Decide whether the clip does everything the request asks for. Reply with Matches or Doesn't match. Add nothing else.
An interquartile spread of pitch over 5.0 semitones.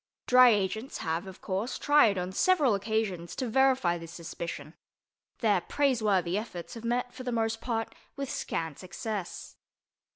Matches